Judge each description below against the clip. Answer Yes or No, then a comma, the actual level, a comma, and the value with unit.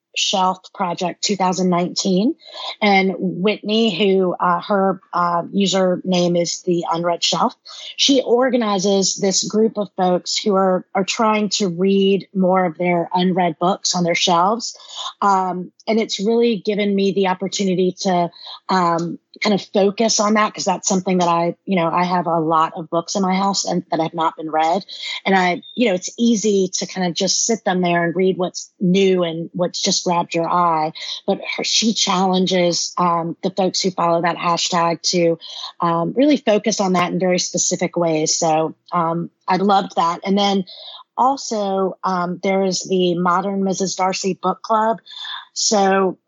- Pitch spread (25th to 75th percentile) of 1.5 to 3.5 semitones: Yes, narrow, 2.4 semitones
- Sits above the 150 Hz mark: Yes, medium, 185 Hz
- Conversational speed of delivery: Yes, average, 170 wpm